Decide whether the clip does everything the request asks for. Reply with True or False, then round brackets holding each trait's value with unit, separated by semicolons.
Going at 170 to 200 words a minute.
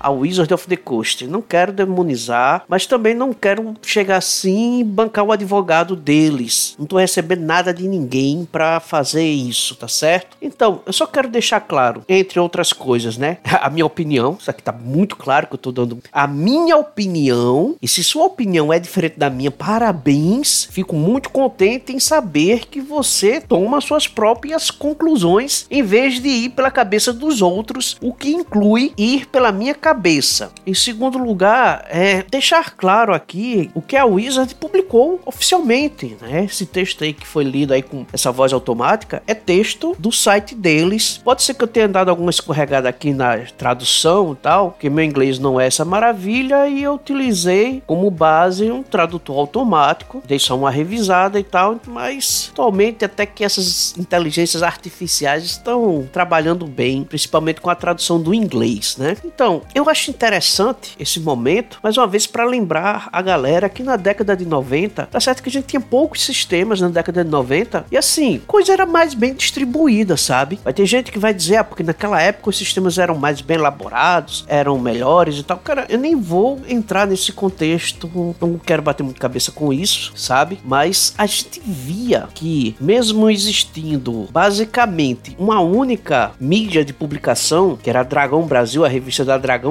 True (180 wpm)